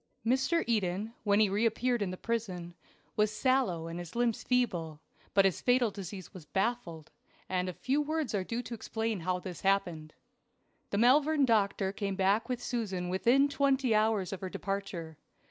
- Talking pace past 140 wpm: Yes, average, 170 wpm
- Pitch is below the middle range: No, high, 205 Hz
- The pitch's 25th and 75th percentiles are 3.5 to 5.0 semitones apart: Yes, average, 4.7 semitones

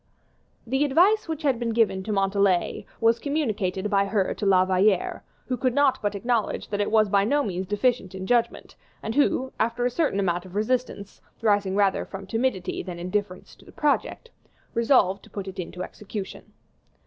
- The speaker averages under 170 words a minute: No, average, 185 wpm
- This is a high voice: Yes, high, 210 Hz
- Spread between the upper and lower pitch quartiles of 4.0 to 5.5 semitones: Yes, average, 4.3 semitones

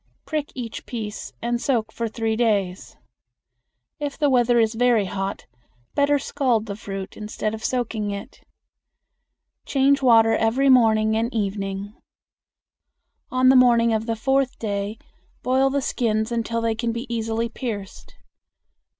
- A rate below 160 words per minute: Yes, average, 140 wpm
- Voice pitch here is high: Yes, high, 230 Hz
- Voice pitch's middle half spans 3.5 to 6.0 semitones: No, narrow, 2.6 semitones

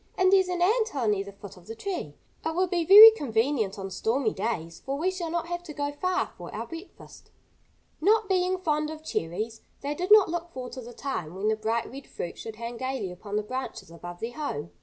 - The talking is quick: Yes, fast, 230 wpm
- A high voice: Yes, very high, 270 Hz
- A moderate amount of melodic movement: No, wide, 8.3 semitones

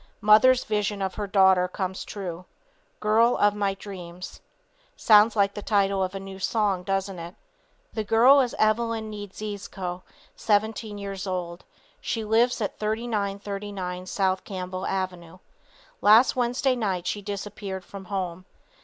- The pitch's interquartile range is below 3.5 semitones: Yes, narrow, 2.4 semitones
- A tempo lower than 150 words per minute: Yes, slow, 135 wpm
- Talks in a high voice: Yes, high, 200 Hz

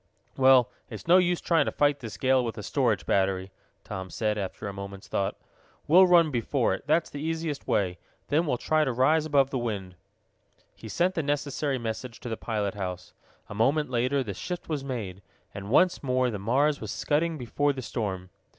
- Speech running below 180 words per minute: No, average, 195 wpm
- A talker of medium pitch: No, low, 130 Hz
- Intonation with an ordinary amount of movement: No, wide, 6.0 semitones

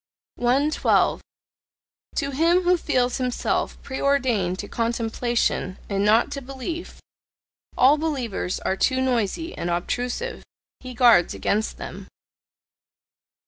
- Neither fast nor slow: No, slow, 105 wpm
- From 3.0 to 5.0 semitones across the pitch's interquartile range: Yes, average, 4.1 semitones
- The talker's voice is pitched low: No, very high, 250 Hz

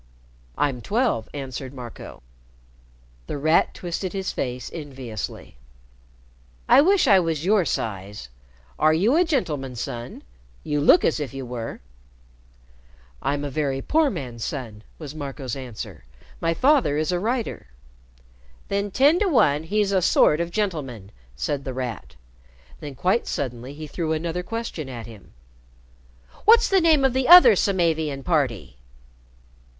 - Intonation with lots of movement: Yes, wide, 7.4 semitones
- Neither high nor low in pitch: Yes, medium, 155 Hz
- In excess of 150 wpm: No, average, 140 wpm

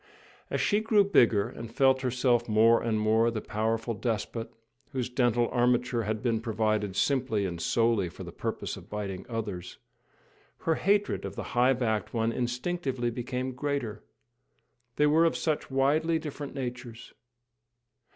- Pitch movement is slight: No, average, 3.2 semitones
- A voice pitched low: Yes, low, 120 Hz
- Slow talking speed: No, average, 150 wpm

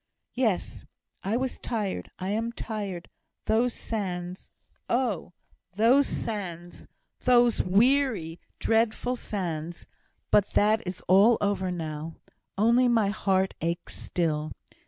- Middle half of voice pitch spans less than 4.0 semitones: No, average, 4.7 semitones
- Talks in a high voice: Yes, high, 205 Hz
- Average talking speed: No, slow, 110 wpm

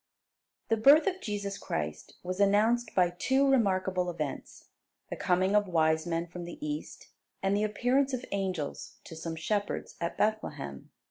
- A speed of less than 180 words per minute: Yes, average, 155 wpm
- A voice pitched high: Yes, high, 195 Hz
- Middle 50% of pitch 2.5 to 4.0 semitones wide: No, average, 4.7 semitones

